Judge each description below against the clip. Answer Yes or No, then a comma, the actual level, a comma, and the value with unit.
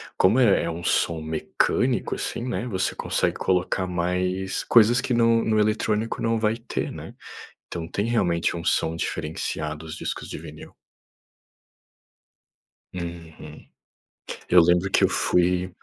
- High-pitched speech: No, very low, 90 Hz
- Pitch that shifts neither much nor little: Yes, average, 4.5 semitones